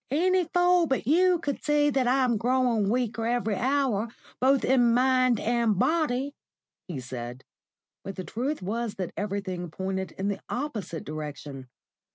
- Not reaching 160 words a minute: Yes, average, 150 wpm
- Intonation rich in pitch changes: Yes, wide, 5.9 semitones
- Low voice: No, high, 235 Hz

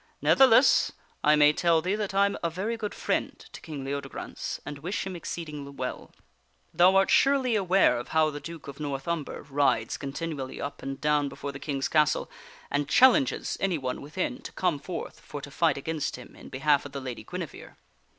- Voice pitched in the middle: Yes, medium, 150 Hz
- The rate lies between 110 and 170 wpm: No, average, 190 wpm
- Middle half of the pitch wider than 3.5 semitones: Yes, average, 4.7 semitones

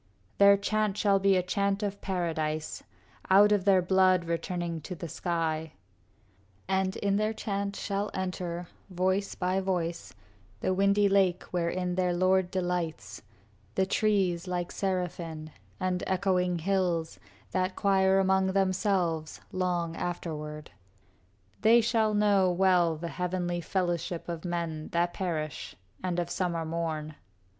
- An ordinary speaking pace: No, slow, 130 wpm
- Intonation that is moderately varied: No, narrow, 2.3 semitones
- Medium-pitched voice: Yes, medium, 180 Hz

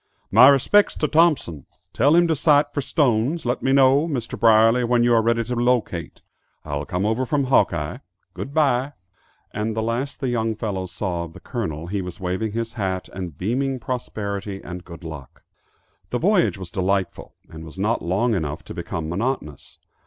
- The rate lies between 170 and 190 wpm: Yes, average, 180 wpm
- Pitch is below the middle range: Yes, low, 115 Hz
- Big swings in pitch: Yes, wide, 6.0 semitones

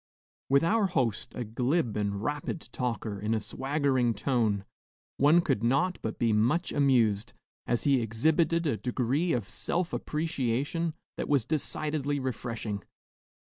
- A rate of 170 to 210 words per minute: No, slow, 135 wpm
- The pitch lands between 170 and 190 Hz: No, low, 130 Hz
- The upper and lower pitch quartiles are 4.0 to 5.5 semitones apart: Yes, average, 5.1 semitones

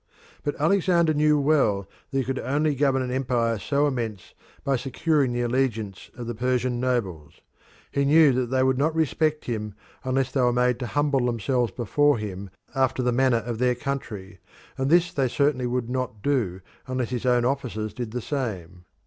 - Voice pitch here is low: Yes, low, 125 Hz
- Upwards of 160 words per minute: Yes, average, 185 wpm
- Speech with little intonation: No, average, 3.0 semitones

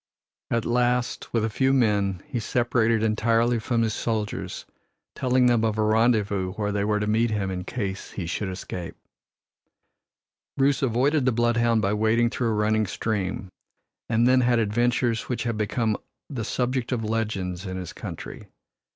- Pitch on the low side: Yes, low, 110 Hz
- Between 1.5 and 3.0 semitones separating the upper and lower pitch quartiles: Yes, narrow, 2.5 semitones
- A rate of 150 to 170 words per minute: Yes, average, 165 wpm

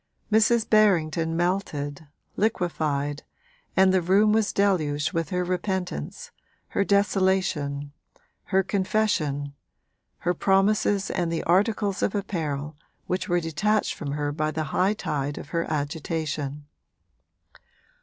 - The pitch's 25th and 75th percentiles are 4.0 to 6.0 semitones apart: Yes, average, 4.8 semitones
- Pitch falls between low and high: Yes, medium, 175 Hz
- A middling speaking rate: No, slow, 115 wpm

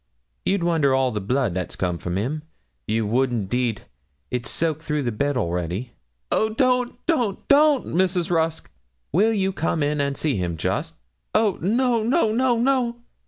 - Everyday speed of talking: Yes, average, 165 wpm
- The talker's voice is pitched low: No, medium, 155 Hz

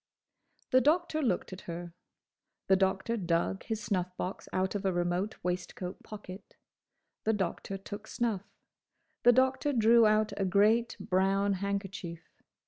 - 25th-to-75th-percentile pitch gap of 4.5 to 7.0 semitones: No, average, 3.2 semitones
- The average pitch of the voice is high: Yes, high, 195 Hz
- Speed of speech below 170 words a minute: Yes, slow, 135 wpm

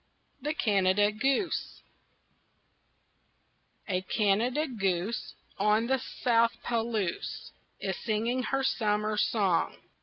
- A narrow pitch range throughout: No, average, 3.4 semitones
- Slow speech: Yes, slow, 90 wpm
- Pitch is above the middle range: Yes, high, 215 Hz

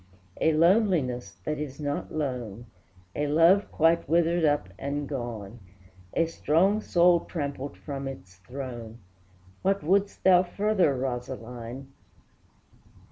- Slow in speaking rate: Yes, slow, 115 wpm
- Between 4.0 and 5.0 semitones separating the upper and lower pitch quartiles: No, wide, 5.4 semitones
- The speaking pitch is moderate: Yes, medium, 145 Hz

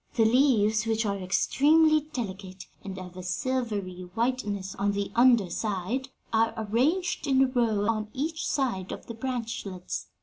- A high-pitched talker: Yes, high, 220 Hz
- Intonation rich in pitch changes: No, average, 4.7 semitones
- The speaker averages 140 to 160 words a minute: Yes, average, 155 wpm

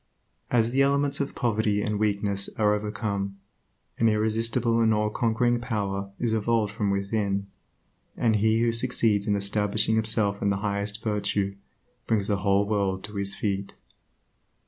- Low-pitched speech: Yes, low, 105 Hz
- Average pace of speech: Yes, average, 145 wpm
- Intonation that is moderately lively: No, narrow, 2.1 semitones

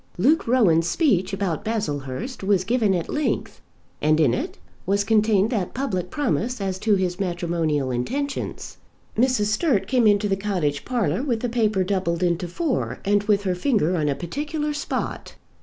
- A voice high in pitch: Yes, high, 200 Hz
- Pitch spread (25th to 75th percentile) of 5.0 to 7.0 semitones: Yes, wide, 5.5 semitones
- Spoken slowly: No, average, 165 wpm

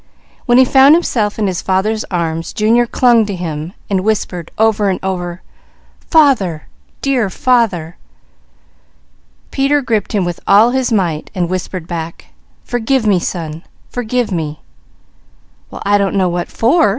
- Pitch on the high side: Yes, high, 200 Hz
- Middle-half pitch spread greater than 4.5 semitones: Yes, wide, 5.4 semitones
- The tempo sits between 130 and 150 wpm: Yes, average, 145 wpm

